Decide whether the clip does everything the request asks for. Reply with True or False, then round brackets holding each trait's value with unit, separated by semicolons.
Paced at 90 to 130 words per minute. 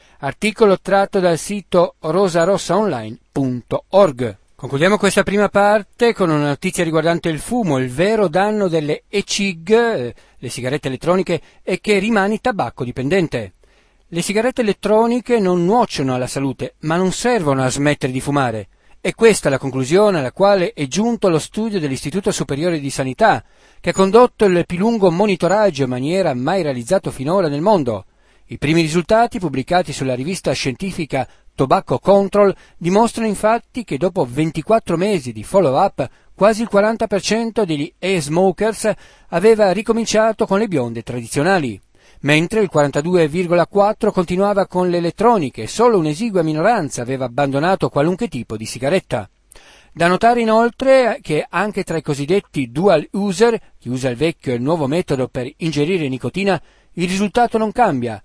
False (145 wpm)